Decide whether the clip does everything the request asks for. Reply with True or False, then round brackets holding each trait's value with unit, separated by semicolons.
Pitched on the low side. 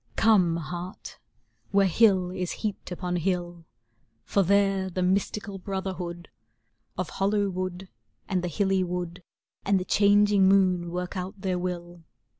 False (185 Hz)